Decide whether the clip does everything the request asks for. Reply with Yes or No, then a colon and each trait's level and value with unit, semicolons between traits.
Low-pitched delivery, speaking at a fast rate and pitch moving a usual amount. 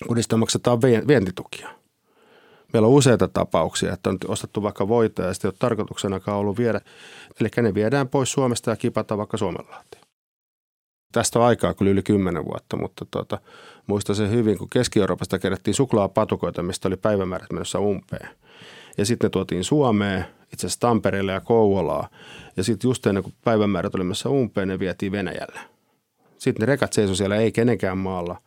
Yes: low, 105 Hz; fast, 160 wpm; average, 3.2 semitones